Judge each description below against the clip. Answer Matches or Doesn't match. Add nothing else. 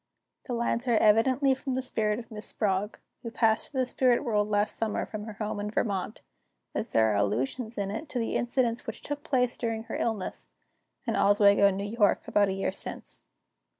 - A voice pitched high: Matches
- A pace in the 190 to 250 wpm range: Matches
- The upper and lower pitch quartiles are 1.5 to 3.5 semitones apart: Matches